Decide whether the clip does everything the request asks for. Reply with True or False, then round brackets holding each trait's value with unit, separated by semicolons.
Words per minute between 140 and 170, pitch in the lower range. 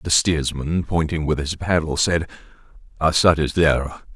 True (145 wpm; 80 Hz)